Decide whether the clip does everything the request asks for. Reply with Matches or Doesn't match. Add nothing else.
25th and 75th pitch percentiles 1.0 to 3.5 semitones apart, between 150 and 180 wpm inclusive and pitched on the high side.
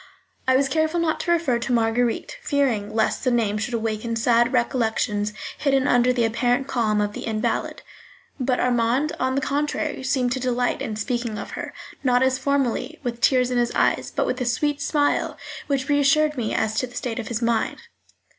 Doesn't match